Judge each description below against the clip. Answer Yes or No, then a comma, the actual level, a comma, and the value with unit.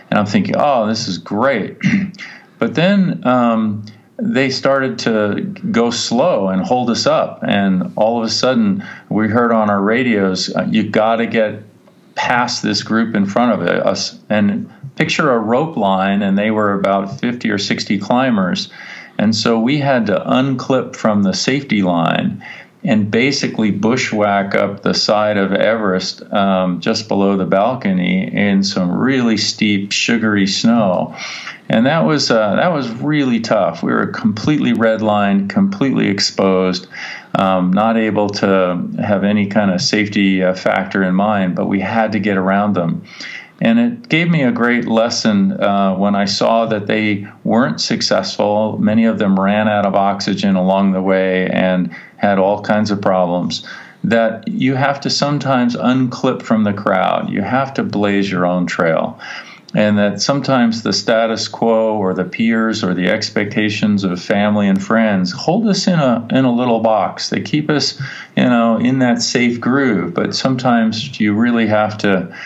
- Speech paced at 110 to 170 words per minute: Yes, average, 165 wpm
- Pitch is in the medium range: No, low, 110 Hz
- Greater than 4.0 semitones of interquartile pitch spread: Yes, average, 4.4 semitones